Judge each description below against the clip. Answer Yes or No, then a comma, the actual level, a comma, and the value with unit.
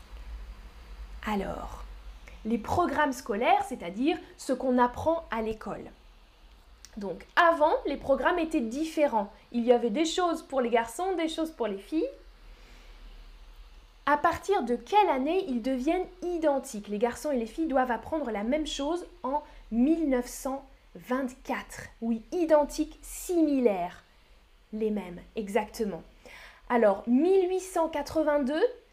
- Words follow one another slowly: Yes, slow, 120 wpm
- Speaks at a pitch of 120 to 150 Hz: No, very high, 275 Hz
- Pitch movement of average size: No, wide, 5.8 semitones